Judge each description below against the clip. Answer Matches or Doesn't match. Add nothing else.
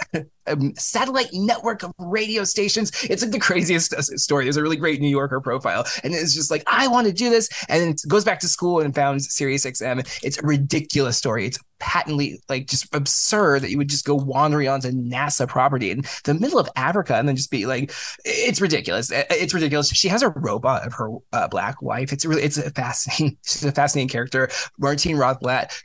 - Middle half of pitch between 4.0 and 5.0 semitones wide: Matches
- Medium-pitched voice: Matches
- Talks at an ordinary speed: Doesn't match